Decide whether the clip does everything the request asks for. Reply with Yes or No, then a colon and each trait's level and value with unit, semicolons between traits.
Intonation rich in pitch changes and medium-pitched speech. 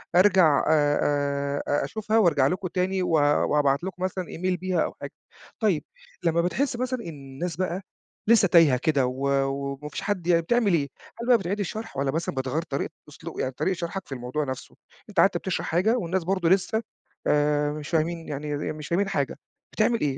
No: average, 4.8 semitones; medium, 170 Hz